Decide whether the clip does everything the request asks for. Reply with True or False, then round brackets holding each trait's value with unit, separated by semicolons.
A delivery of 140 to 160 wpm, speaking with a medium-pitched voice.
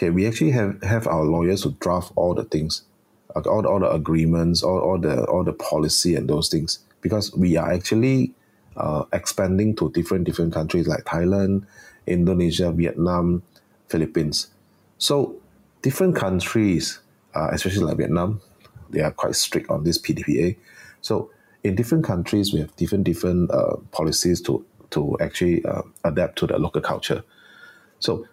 False (155 wpm; 90 Hz)